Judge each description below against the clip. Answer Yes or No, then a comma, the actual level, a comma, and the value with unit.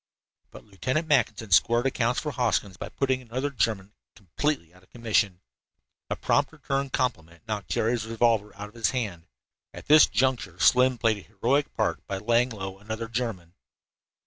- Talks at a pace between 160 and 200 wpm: Yes, average, 165 wpm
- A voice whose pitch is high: No, low, 115 Hz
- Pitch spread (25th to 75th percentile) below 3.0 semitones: No, average, 4.2 semitones